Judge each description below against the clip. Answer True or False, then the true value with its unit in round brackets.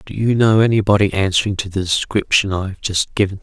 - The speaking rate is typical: False (210 wpm)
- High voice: False (100 Hz)